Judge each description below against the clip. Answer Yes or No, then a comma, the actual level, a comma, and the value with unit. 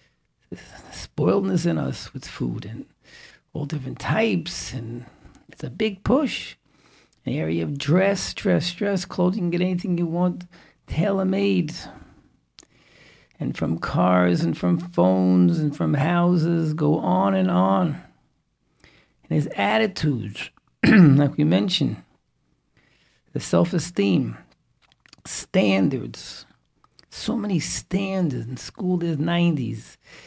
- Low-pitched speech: No, medium, 170 Hz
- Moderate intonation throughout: No, wide, 6.6 semitones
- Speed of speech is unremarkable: No, slow, 115 wpm